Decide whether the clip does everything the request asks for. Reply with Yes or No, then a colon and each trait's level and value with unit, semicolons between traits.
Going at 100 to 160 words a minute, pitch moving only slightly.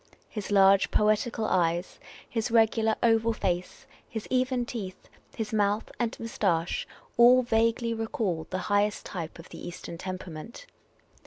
No: slow, 135 wpm; average, 3.6 semitones